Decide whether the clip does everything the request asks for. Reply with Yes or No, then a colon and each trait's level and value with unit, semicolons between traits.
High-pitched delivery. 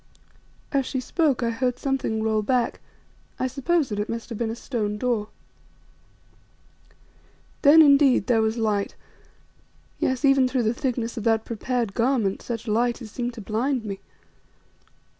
Yes: high, 240 Hz